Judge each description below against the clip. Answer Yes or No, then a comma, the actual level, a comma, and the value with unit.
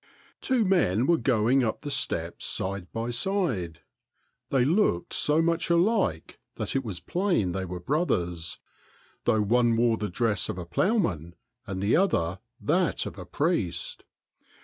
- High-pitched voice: No, low, 115 Hz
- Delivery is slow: No, average, 155 wpm